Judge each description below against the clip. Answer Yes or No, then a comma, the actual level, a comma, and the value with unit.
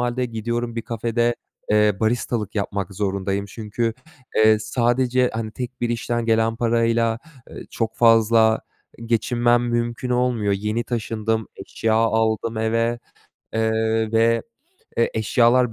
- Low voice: Yes, low, 115 Hz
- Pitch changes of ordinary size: No, narrow, 1.3 semitones